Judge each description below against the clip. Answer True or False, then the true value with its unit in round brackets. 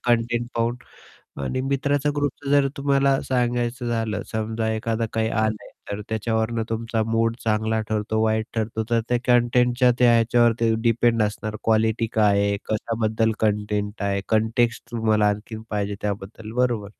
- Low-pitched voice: True (115 Hz)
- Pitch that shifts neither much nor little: False (1.7 semitones)